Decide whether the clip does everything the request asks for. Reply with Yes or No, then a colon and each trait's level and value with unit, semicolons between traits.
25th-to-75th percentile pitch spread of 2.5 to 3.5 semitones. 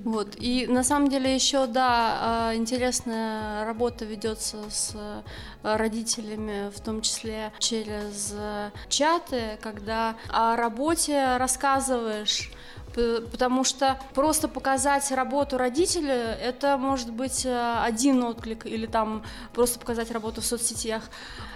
Yes: average, 2.9 semitones